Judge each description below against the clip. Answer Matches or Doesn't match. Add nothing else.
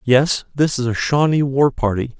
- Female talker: Doesn't match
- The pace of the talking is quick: Doesn't match